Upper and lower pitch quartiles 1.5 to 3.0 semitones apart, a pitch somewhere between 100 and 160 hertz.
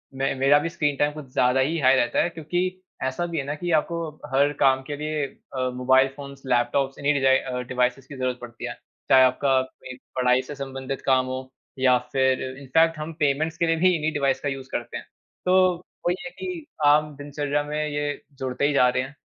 Yes: narrow, 2.5 semitones; medium, 140 Hz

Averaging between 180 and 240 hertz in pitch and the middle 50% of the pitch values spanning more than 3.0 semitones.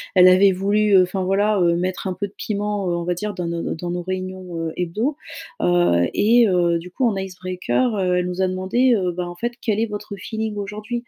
No: medium, 185 Hz; average, 2.7 semitones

